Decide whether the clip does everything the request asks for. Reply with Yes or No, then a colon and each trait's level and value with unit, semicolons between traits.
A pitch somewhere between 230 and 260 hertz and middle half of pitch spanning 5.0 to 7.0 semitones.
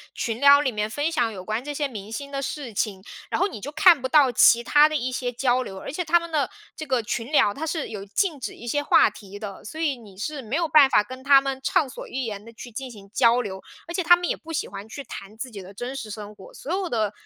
Yes: very high, 255 Hz; wide, 5.4 semitones